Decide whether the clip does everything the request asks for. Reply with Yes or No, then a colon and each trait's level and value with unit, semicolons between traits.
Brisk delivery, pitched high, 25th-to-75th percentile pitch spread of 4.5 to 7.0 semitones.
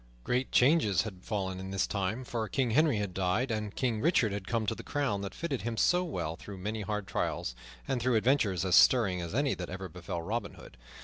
No: fast, 225 wpm; low, 105 Hz; average, 4.8 semitones